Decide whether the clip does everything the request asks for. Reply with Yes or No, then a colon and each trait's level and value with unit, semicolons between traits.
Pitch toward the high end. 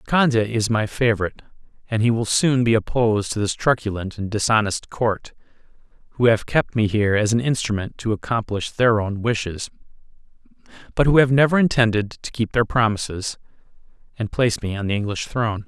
No: low, 110 Hz